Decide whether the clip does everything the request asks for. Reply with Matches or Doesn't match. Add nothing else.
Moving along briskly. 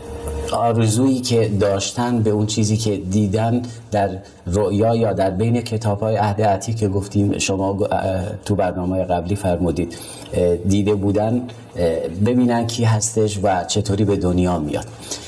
Doesn't match